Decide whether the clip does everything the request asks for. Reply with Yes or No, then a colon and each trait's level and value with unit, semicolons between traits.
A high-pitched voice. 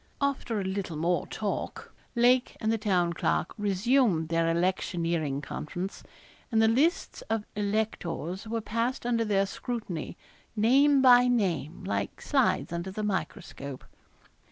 Yes: high, 205 Hz